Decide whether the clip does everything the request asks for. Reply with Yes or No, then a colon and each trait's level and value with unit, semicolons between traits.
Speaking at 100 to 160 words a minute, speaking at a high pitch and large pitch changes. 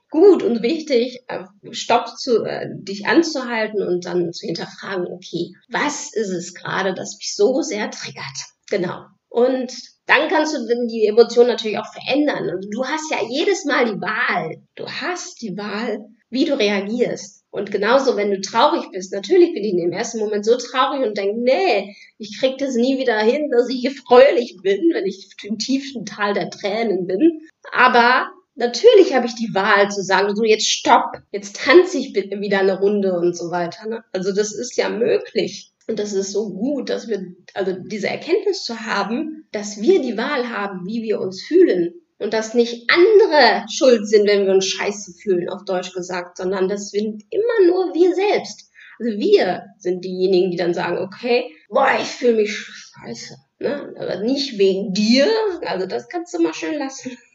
No: average, 185 wpm; high, 230 Hz; wide, 5.7 semitones